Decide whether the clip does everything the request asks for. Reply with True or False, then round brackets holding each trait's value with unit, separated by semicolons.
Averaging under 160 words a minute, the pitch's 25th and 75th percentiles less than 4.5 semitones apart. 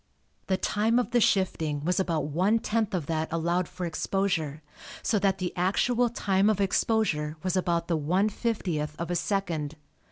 False (170 wpm; 4.1 semitones)